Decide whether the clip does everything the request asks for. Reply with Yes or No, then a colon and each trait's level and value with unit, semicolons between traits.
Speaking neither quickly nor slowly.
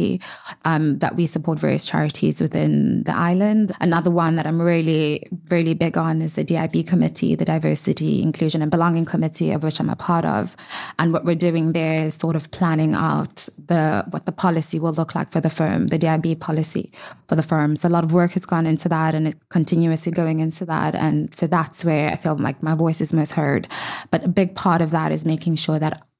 No: fast, 220 wpm